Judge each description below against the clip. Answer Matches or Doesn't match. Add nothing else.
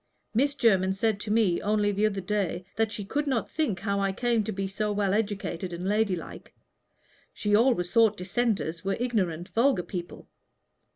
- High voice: Matches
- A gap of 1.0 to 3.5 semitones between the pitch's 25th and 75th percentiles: Matches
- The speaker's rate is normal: Matches